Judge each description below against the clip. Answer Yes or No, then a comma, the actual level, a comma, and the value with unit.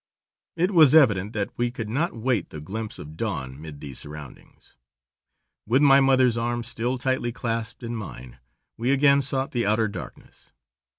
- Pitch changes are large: No, average, 4.7 semitones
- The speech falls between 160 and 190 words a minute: Yes, average, 165 wpm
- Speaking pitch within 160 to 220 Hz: No, low, 115 Hz